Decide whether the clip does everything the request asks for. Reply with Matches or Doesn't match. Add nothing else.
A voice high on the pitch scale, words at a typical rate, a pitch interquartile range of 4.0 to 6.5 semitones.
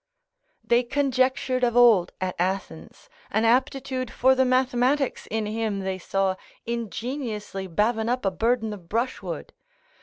Doesn't match